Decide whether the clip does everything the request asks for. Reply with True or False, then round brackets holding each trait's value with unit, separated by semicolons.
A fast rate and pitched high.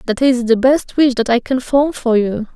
True (260 wpm; 250 Hz)